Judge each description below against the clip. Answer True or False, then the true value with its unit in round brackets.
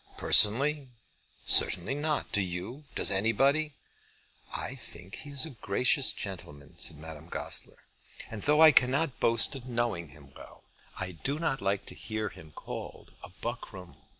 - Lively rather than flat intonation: True (7.1 semitones)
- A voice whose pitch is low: True (115 Hz)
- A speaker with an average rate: True (150 wpm)